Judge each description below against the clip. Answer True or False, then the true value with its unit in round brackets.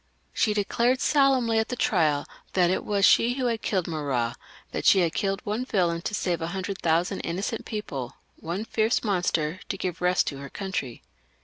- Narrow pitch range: False (4.7 semitones)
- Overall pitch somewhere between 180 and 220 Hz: True (190 Hz)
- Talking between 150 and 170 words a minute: False (185 wpm)